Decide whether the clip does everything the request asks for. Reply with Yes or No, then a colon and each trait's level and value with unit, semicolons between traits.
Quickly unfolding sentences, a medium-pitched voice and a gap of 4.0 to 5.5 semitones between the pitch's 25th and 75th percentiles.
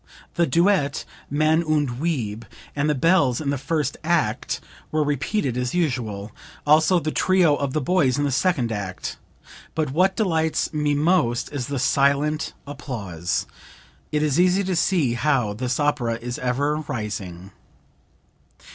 No: average, 145 wpm; medium, 145 Hz; average, 4.4 semitones